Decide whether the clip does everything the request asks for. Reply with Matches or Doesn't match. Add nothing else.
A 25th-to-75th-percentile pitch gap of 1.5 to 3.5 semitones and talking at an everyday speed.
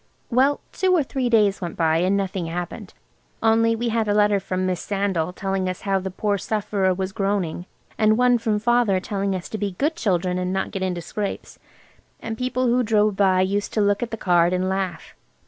Doesn't match